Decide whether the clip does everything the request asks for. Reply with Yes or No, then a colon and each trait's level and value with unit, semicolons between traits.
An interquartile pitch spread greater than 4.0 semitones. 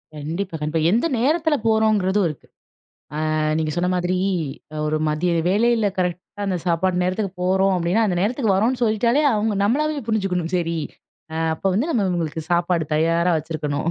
Yes: average, 4.6 semitones